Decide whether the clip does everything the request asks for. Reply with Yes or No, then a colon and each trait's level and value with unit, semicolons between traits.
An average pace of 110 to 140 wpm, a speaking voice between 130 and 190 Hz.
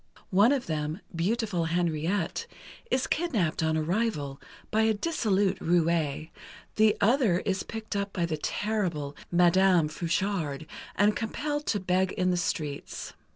Yes: slow, 135 wpm; medium, 185 Hz